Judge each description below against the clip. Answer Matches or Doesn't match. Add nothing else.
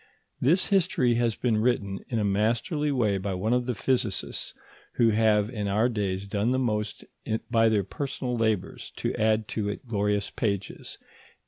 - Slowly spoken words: Doesn't match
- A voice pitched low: Matches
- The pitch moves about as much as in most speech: Matches